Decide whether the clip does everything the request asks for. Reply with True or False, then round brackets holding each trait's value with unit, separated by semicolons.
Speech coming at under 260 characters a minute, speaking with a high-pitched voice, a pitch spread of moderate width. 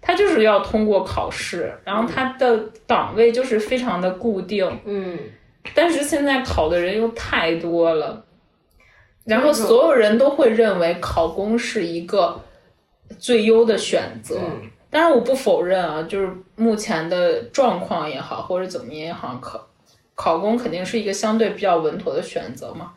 True (245 characters per minute; 220 Hz; 4.5 semitones)